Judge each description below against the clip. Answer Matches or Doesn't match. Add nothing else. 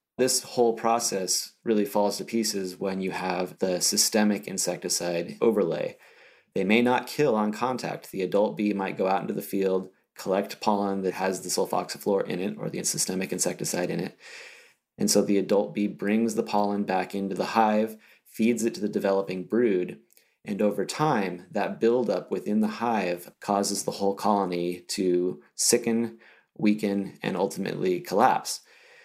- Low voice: Matches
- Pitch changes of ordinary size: Matches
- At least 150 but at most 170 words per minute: Matches